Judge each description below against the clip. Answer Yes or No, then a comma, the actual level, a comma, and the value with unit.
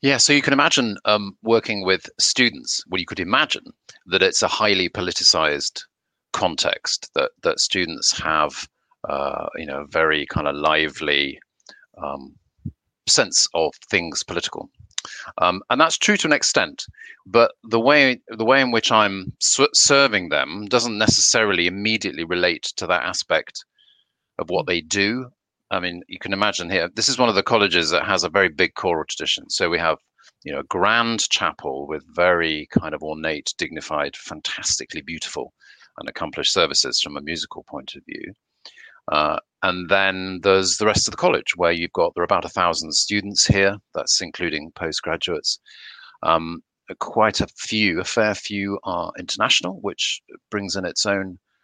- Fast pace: No, average, 165 wpm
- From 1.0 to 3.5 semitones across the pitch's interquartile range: No, average, 4.3 semitones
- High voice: No, low, 105 Hz